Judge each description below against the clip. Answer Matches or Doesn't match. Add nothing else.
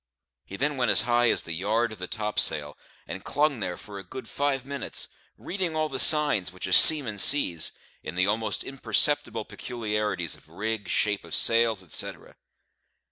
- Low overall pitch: Matches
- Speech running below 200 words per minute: Matches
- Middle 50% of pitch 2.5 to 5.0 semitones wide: Doesn't match